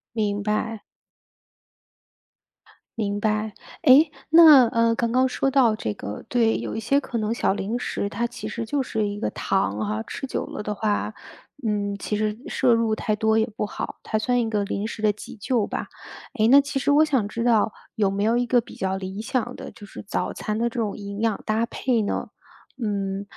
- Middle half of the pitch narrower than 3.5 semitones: Yes, narrow, 2.6 semitones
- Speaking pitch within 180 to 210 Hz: No, high, 220 Hz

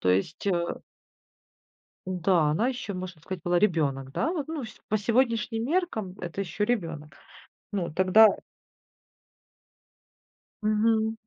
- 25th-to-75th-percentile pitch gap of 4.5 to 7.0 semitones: Yes, average, 4.9 semitones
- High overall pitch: Yes, high, 195 Hz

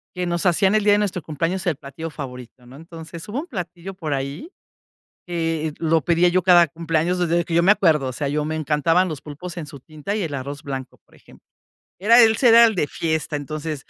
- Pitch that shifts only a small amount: No, average, 3.4 semitones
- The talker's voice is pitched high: No, medium, 165 Hz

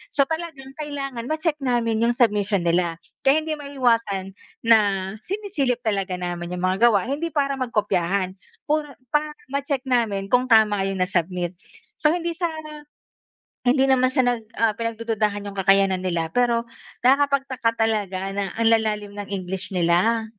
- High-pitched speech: Yes, high, 230 Hz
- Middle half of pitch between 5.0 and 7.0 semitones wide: Yes, wide, 5.6 semitones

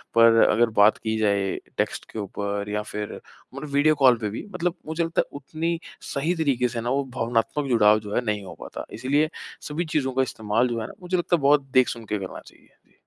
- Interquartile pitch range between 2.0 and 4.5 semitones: No, wide, 5.6 semitones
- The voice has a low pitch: Yes, low, 120 Hz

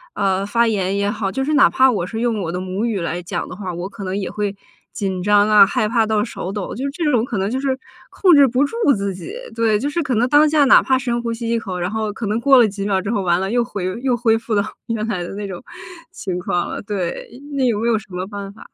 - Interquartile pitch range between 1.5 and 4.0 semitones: Yes, average, 3.7 semitones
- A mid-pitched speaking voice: No, high, 215 Hz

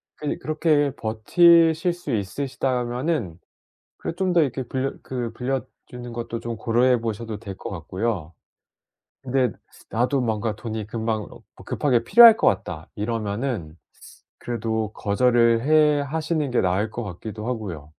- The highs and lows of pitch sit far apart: No, average, 4.2 semitones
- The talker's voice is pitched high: No, low, 120 Hz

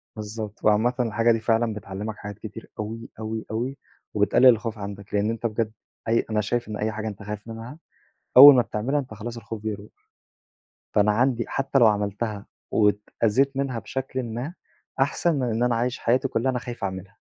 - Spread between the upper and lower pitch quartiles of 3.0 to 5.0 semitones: No, narrow, 2.6 semitones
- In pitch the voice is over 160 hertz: No, low, 115 Hz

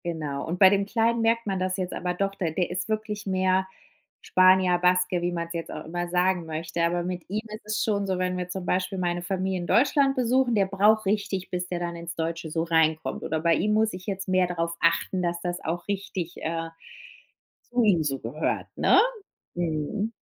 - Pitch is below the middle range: No, medium, 180 Hz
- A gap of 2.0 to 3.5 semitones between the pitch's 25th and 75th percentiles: Yes, average, 2.7 semitones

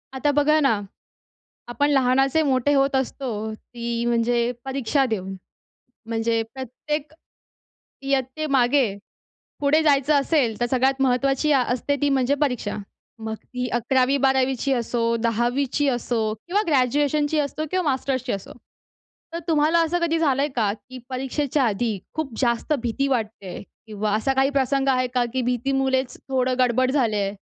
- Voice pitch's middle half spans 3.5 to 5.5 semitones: No, average, 2.9 semitones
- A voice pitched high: Yes, very high, 260 Hz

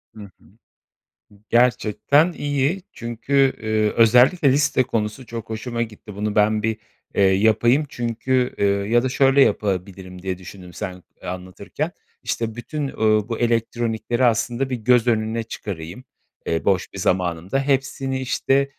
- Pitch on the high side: No, low, 115 Hz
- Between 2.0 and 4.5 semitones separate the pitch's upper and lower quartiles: Yes, average, 4.2 semitones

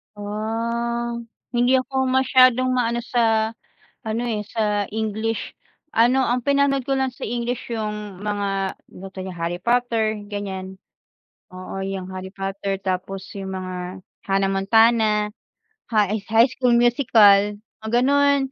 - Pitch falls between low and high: No, high, 220 Hz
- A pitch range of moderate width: Yes, average, 3.6 semitones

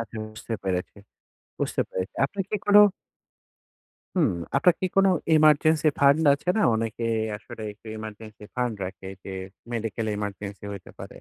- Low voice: Yes, low, 115 Hz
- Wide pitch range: Yes, wide, 6.8 semitones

